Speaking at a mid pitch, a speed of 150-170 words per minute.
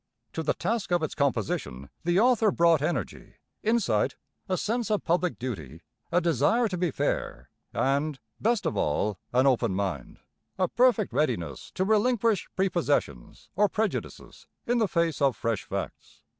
Yes: medium, 170 Hz; average, 155 wpm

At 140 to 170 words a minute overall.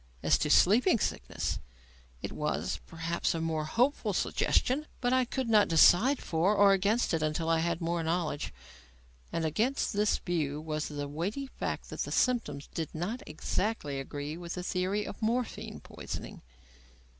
Yes: average, 155 wpm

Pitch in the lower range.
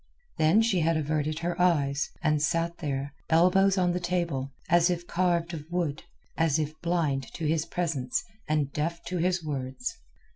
No: medium, 165 Hz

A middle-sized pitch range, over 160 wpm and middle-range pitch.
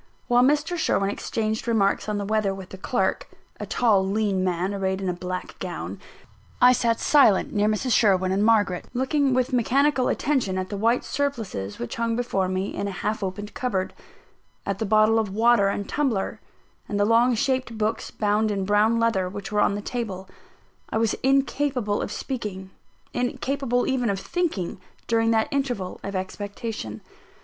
No: average, 3.9 semitones; average, 175 wpm; high, 215 Hz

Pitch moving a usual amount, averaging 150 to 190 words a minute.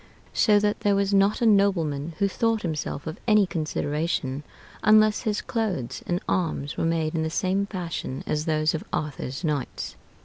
Yes: average, 4.8 semitones; average, 170 wpm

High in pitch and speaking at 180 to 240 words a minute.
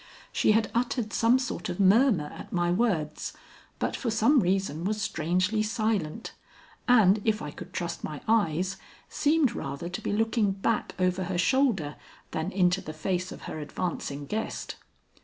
No: high, 195 Hz; average, 160 wpm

